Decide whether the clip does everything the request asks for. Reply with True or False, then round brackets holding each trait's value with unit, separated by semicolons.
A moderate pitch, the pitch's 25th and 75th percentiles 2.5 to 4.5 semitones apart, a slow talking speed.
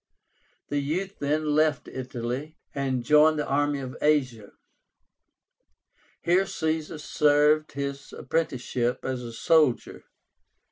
True (145 Hz; 3.0 semitones; 105 wpm)